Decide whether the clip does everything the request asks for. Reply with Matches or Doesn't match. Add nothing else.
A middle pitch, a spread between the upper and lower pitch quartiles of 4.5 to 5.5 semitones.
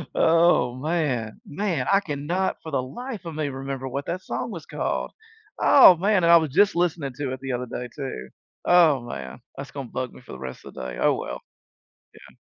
Matches